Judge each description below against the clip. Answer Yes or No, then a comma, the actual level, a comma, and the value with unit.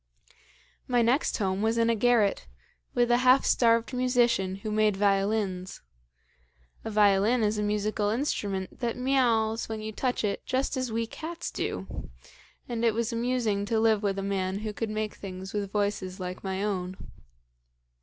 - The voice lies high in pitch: Yes, high, 215 Hz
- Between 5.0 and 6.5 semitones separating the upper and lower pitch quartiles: No, average, 2.9 semitones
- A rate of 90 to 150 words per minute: No, average, 165 wpm